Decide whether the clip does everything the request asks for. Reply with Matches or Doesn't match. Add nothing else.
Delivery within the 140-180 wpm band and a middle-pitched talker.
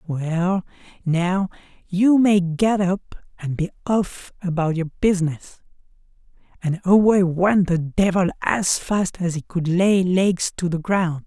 Matches